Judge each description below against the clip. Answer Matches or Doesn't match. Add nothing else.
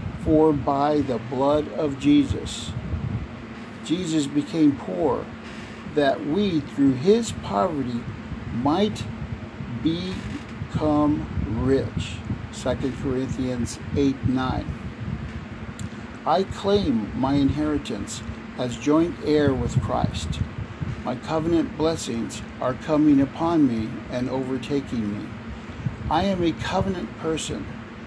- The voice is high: Doesn't match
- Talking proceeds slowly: Matches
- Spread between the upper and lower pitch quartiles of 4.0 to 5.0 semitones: Matches